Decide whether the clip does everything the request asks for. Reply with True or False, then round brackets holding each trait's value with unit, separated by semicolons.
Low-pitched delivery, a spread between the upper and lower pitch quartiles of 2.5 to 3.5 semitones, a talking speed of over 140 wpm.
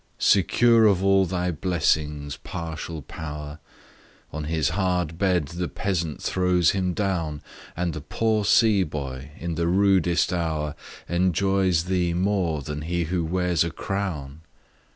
False (85 Hz; 3.2 semitones; 135 wpm)